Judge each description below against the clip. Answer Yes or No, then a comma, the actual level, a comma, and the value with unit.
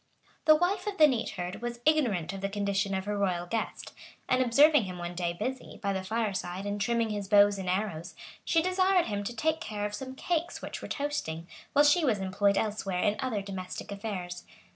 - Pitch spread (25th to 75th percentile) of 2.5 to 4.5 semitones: No, wide, 5.4 semitones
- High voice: Yes, high, 205 Hz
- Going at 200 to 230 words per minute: Yes, fast, 205 wpm